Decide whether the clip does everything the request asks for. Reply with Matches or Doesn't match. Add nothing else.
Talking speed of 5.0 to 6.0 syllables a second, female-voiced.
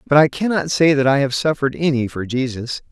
Doesn't match